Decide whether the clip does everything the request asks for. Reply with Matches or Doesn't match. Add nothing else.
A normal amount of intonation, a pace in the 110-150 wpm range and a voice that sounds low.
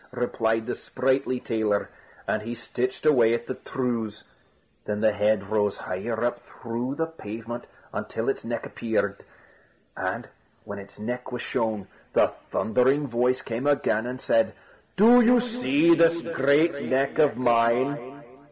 Matches